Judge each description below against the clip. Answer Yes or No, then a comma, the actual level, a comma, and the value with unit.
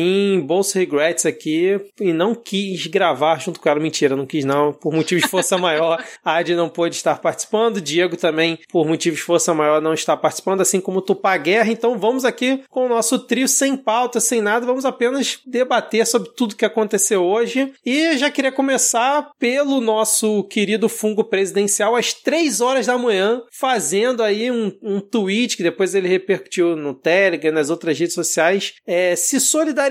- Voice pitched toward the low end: No, high, 200 Hz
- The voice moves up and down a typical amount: No, wide, 5.8 semitones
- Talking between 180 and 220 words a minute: Yes, fast, 185 wpm